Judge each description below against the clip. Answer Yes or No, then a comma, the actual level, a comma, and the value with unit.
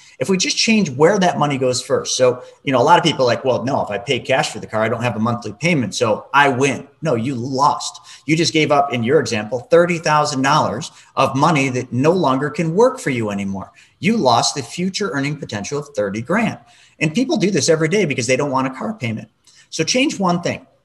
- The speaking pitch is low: No, medium, 145 Hz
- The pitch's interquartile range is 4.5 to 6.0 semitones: Yes, wide, 5.5 semitones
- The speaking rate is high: Yes, fast, 240 wpm